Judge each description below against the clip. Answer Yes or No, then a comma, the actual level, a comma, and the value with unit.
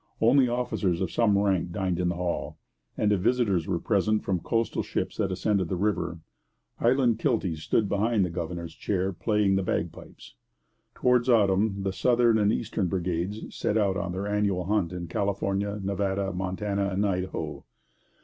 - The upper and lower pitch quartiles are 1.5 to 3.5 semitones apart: Yes, average, 2.8 semitones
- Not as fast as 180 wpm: Yes, average, 165 wpm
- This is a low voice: Yes, low, 100 Hz